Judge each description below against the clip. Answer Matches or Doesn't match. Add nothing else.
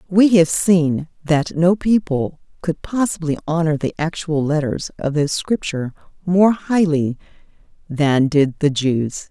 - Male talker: Doesn't match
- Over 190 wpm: Doesn't match